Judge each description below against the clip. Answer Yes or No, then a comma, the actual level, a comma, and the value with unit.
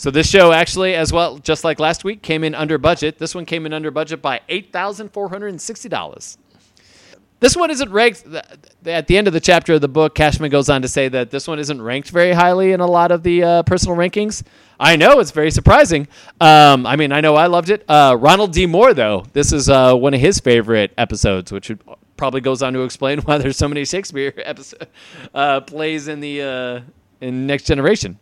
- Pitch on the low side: No, medium, 155 Hz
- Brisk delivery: Yes, fast, 215 wpm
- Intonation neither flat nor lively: Yes, average, 4.2 semitones